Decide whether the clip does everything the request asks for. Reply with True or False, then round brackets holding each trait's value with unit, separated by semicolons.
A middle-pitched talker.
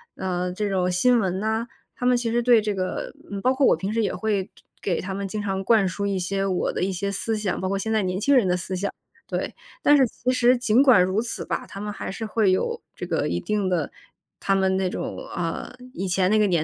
False (200 Hz)